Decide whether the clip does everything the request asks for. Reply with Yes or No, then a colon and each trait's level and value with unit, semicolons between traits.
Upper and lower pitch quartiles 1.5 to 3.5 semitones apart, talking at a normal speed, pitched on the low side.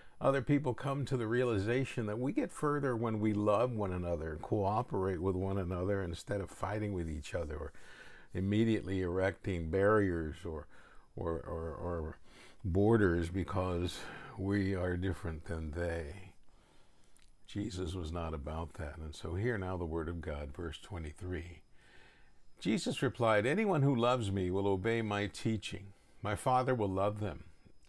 No: average, 4.2 semitones; average, 150 wpm; very low, 95 Hz